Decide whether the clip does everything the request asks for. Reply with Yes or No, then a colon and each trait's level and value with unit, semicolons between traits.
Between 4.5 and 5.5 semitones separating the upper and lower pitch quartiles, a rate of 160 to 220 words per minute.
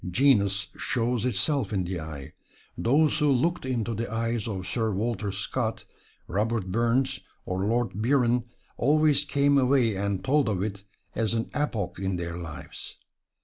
No: average, 4.9 semitones; average, 150 wpm